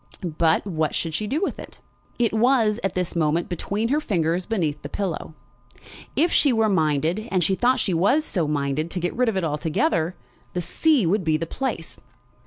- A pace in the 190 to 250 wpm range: Yes, average, 195 wpm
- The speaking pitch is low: No, medium, 180 Hz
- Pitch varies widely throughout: Yes, wide, 5.7 semitones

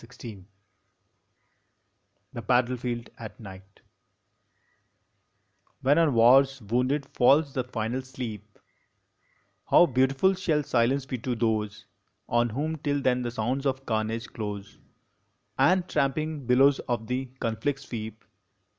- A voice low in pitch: Yes, low, 125 Hz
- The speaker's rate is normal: No, slow, 130 wpm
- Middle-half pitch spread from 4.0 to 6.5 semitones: No, average, 3.4 semitones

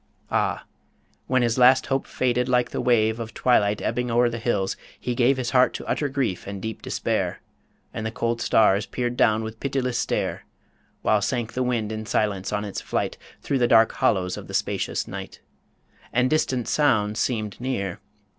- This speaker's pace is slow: No, average, 185 wpm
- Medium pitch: No, low, 120 Hz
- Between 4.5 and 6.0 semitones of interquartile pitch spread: No, average, 2.8 semitones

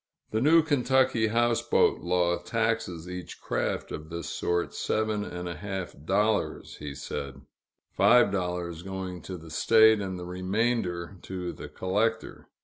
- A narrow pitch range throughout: No, average, 4.2 semitones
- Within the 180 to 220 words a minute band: No, average, 145 wpm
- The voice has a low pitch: Yes, very low, 95 Hz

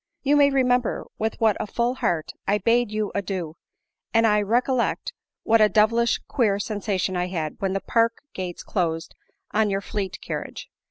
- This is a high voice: Yes, high, 210 Hz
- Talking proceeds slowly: No, average, 170 wpm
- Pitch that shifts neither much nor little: Yes, average, 3.4 semitones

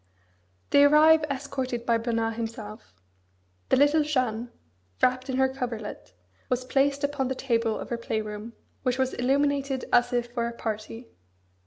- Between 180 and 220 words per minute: No, average, 155 wpm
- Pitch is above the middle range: Yes, very high, 250 Hz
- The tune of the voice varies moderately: Yes, average, 3.1 semitones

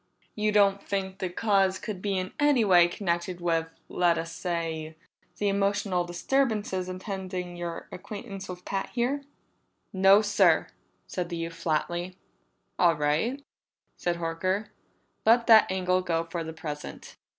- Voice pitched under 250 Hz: Yes, medium, 185 Hz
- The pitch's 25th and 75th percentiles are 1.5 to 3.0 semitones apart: Yes, average, 2.7 semitones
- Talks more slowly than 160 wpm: Yes, average, 140 wpm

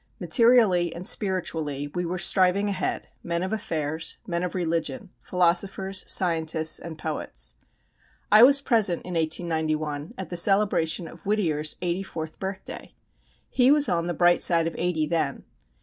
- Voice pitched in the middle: Yes, medium, 175 Hz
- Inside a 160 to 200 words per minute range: No, average, 150 wpm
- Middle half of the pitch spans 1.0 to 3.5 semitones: Yes, average, 3.2 semitones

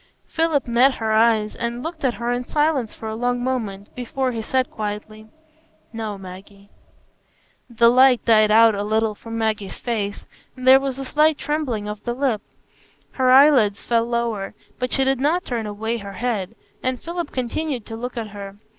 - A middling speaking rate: Yes, average, 180 wpm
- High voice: Yes, high, 235 Hz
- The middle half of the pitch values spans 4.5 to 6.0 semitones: No, average, 3.4 semitones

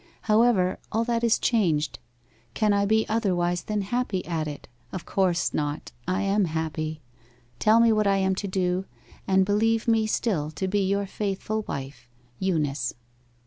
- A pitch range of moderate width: Yes, average, 3.8 semitones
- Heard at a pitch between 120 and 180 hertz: No, high, 195 Hz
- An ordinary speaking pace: Yes, average, 160 wpm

